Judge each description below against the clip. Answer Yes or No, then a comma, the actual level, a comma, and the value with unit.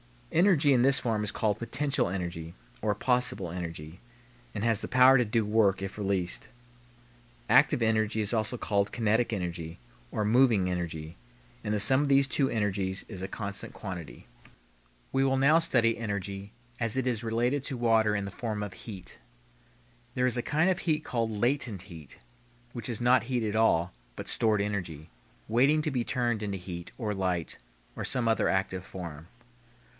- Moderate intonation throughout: Yes, average, 4.4 semitones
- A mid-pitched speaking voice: No, low, 110 Hz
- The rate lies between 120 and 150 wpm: No, average, 165 wpm